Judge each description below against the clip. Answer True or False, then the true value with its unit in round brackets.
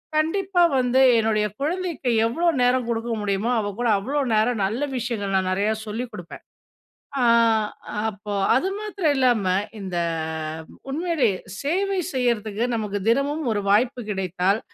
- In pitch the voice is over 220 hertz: True (240 Hz)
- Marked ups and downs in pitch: True (5.9 semitones)